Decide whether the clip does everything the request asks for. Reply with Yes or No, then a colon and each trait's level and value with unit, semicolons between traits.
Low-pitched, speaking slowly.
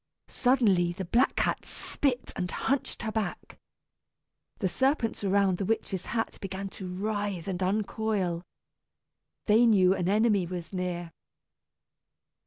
No: high, 195 Hz; slow, 125 wpm